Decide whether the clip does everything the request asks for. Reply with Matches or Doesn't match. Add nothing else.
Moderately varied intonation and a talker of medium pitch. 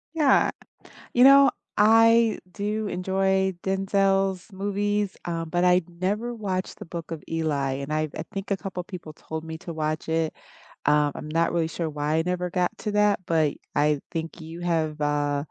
Matches